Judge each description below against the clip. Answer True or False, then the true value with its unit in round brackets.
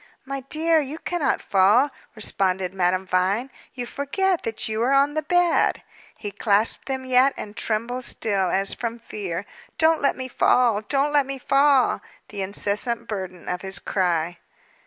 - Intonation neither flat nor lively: False (6.0 semitones)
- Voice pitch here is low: False (235 Hz)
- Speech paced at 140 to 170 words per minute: True (160 wpm)